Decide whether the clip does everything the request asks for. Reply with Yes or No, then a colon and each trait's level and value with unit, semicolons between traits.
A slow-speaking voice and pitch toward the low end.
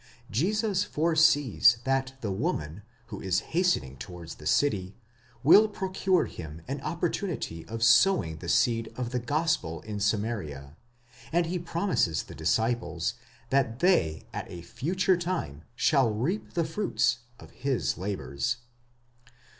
Yes: slow, 130 wpm; low, 120 Hz